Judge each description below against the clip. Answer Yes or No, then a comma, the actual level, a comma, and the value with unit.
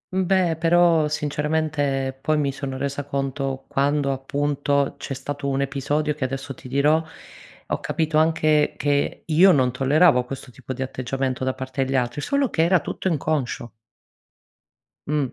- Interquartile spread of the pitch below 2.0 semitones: No, narrow, 2.5 semitones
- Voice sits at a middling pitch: Yes, medium, 145 Hz